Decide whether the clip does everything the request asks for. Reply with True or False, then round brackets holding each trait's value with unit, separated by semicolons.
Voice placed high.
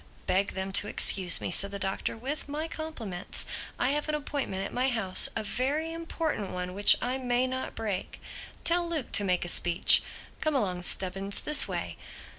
True (225 Hz)